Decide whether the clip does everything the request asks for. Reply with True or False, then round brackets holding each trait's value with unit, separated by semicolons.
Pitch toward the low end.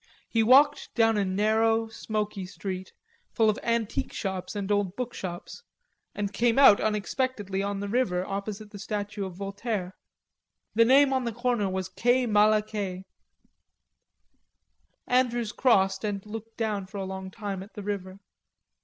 False (210 Hz)